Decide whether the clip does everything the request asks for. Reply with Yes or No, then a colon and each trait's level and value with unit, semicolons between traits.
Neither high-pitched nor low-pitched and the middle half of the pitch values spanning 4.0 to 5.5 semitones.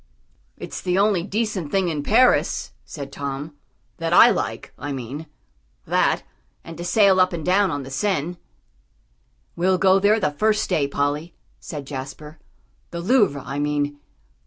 Yes: medium, 165 Hz; average, 5.1 semitones